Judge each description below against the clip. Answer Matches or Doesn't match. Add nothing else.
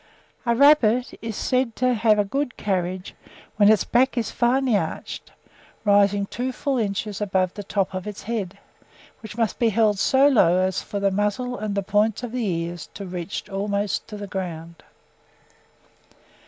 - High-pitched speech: Matches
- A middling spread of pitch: Matches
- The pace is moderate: Matches